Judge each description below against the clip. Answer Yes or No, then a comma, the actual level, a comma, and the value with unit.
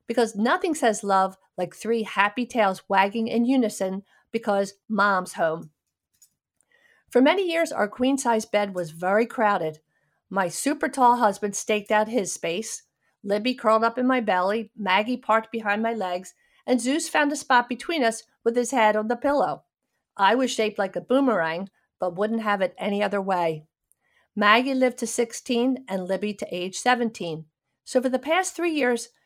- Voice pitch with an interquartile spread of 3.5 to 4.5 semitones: Yes, average, 4.2 semitones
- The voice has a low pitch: No, high, 220 Hz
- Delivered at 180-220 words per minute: No, average, 170 wpm